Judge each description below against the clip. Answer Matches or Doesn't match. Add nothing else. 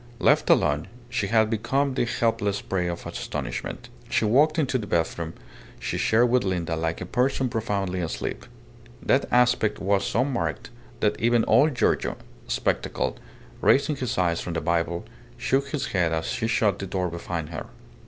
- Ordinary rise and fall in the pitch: Doesn't match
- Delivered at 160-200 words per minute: Matches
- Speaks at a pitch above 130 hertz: Doesn't match